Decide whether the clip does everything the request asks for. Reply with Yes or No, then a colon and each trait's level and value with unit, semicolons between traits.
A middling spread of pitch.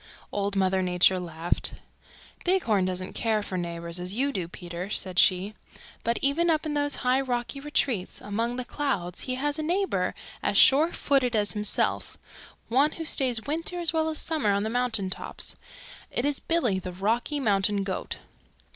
No: wide, 7.3 semitones